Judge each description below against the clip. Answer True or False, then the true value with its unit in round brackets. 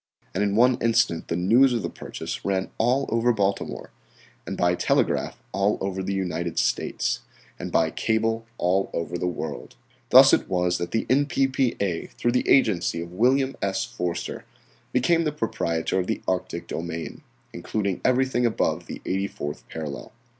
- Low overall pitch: True (100 Hz)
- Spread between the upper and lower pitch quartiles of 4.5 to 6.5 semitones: True (5.5 semitones)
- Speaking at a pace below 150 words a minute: False (165 wpm)